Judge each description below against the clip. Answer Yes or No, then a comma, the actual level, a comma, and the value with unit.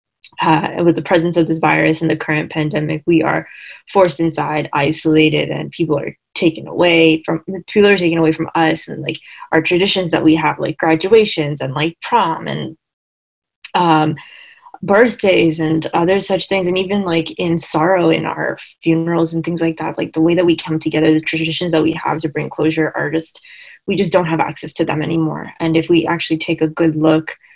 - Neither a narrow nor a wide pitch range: No, narrow, 1.9 semitones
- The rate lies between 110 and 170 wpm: No, average, 200 wpm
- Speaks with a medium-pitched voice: Yes, medium, 165 Hz